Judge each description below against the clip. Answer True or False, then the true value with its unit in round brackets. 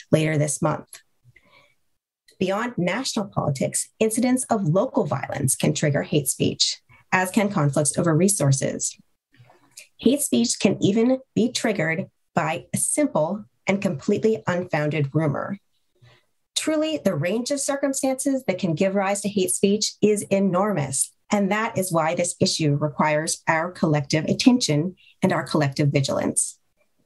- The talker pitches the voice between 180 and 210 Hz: True (190 Hz)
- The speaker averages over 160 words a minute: False (135 wpm)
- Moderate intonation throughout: False (5.8 semitones)